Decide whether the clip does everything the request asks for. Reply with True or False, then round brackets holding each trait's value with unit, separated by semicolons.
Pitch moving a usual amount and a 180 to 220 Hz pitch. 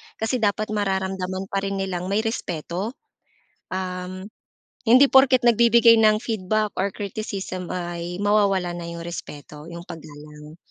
True (3.6 semitones; 190 Hz)